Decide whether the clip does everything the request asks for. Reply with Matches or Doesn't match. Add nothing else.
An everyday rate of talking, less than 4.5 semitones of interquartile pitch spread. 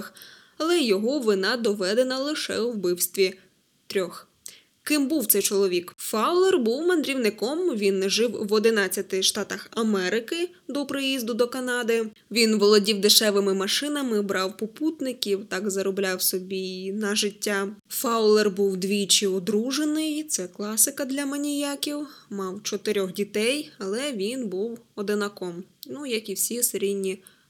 Doesn't match